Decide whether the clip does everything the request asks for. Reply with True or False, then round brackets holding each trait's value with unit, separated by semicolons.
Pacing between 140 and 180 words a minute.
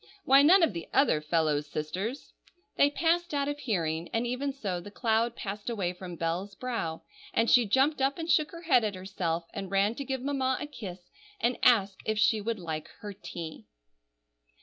False (195 wpm)